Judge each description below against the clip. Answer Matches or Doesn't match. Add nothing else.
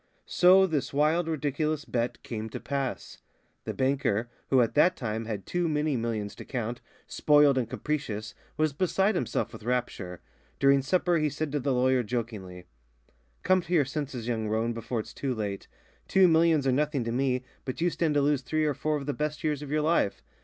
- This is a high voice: Doesn't match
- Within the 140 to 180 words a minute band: Doesn't match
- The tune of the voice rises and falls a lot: Doesn't match